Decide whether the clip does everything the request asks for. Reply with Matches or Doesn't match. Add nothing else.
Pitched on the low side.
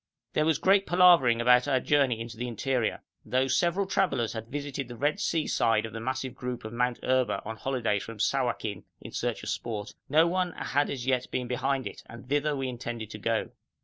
Matches